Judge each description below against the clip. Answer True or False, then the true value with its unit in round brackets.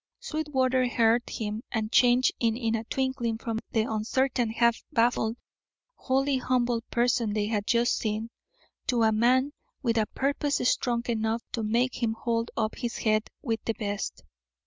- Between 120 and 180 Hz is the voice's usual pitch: False (235 Hz)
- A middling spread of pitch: False (2.2 semitones)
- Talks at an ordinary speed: True (155 wpm)